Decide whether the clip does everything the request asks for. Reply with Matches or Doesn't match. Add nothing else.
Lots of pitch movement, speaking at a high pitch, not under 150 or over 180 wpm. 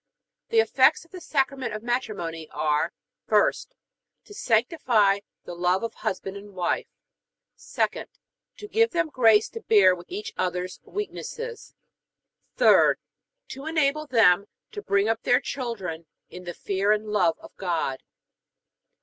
Doesn't match